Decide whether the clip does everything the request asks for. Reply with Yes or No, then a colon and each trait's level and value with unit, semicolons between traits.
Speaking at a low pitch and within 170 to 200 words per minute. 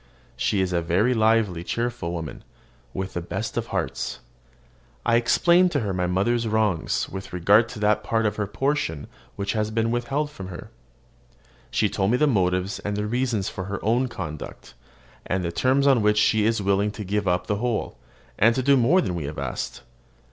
Yes: low, 105 Hz; average, 190 wpm